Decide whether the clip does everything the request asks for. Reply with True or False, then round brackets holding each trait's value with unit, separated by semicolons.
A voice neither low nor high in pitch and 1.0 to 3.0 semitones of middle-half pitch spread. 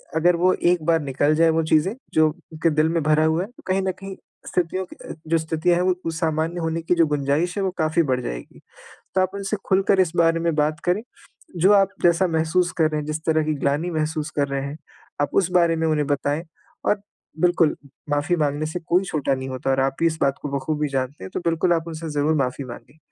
True (160 Hz; 2.7 semitones)